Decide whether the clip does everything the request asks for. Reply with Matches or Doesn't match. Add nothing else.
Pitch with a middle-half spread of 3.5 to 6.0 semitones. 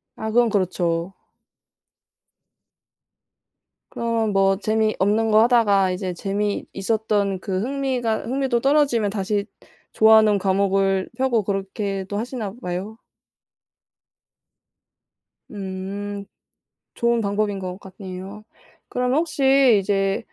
Doesn't match